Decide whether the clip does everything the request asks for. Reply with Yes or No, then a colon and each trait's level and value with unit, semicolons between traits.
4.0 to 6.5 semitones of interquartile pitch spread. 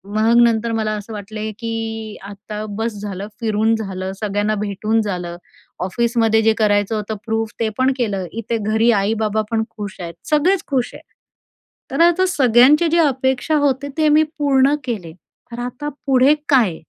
No: average, 3.6 semitones